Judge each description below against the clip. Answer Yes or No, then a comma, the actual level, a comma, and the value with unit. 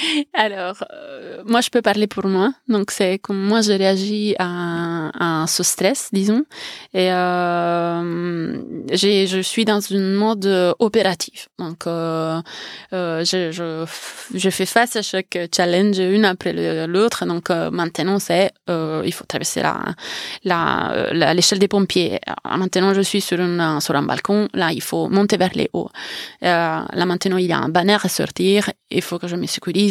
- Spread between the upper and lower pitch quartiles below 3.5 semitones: Yes, average, 2.9 semitones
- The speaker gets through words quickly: No, average, 175 wpm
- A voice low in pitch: No, medium, 185 Hz